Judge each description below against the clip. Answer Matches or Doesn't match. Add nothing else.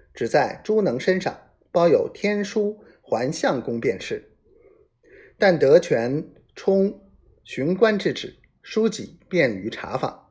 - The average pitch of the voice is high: Matches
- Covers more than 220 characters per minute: Doesn't match